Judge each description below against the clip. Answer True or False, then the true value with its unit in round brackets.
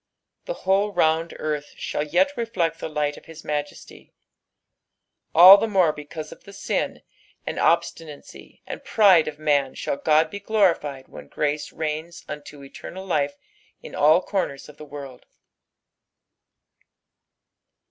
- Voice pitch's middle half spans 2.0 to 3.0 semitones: False (4.2 semitones)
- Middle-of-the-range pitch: True (155 Hz)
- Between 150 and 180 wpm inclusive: False (135 wpm)